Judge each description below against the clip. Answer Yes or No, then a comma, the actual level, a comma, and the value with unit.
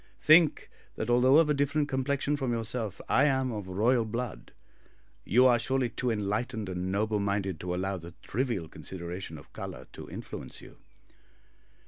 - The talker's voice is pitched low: Yes, low, 115 Hz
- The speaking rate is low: No, average, 160 wpm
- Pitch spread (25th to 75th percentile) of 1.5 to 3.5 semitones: No, average, 5.3 semitones